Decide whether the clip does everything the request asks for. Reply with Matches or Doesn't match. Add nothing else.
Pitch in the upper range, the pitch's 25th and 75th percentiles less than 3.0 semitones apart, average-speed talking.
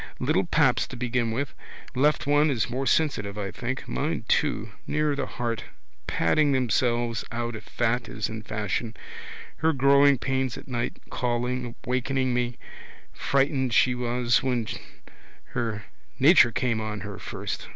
Doesn't match